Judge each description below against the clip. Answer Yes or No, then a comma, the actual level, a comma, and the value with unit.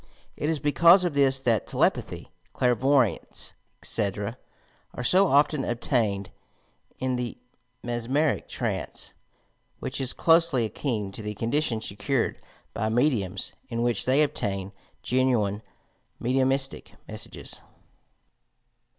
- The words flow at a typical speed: No, slow, 105 wpm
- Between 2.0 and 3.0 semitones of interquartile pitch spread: No, average, 4.2 semitones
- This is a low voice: Yes, low, 125 Hz